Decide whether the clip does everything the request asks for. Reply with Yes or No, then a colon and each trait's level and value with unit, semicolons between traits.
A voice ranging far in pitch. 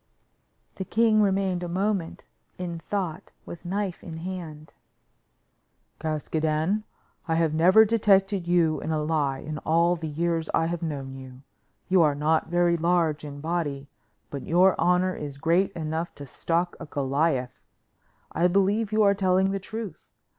No: average, 3.4 semitones